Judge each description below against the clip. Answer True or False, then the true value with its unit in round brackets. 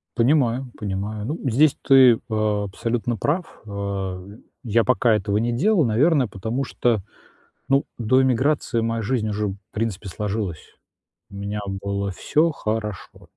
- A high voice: False (110 Hz)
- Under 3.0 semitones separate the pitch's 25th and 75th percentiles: False (4.2 semitones)